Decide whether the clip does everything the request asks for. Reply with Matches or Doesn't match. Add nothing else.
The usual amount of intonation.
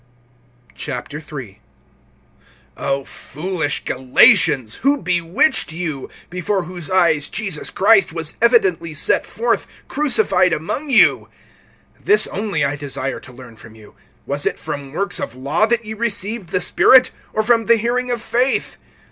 Doesn't match